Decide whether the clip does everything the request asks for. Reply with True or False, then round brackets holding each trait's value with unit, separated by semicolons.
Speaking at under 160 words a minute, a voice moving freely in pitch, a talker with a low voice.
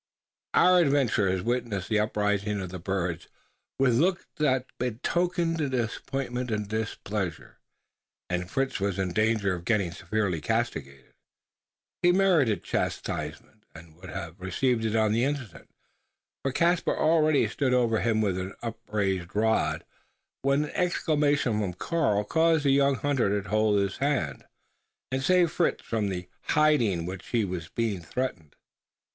True (145 wpm; 6.1 semitones; 110 Hz)